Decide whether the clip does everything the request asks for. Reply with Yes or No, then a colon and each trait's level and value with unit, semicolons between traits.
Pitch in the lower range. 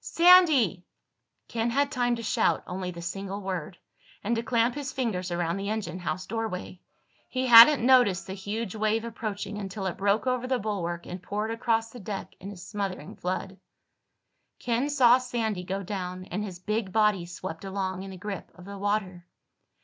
No: high, 205 Hz